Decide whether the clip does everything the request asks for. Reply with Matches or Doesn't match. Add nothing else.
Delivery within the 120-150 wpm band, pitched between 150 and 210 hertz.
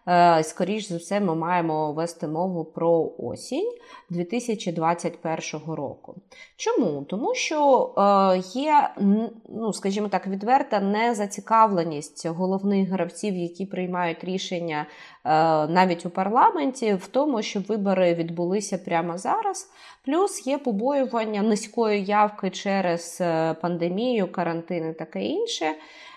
Doesn't match